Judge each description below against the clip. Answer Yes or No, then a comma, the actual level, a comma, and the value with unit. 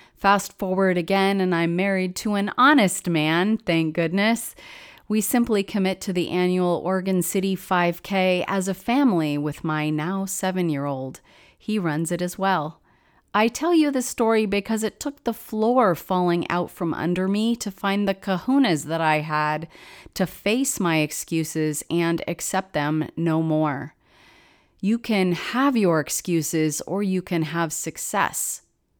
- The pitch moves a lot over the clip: No, average, 4.2 semitones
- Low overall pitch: No, medium, 185 Hz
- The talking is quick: No, average, 155 wpm